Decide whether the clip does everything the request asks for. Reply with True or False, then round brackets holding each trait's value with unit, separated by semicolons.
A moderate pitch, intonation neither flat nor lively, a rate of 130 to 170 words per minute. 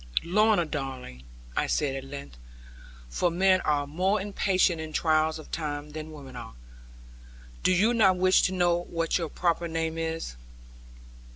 True (165 Hz; 3.9 semitones; 160 wpm)